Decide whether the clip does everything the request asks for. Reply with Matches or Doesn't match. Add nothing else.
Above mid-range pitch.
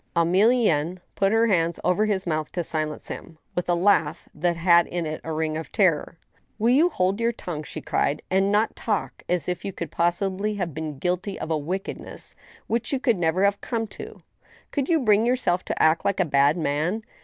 Doesn't match